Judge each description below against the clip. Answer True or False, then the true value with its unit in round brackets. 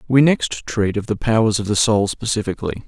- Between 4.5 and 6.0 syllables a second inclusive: True (5.6 syllables/s)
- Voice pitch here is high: False (110 Hz)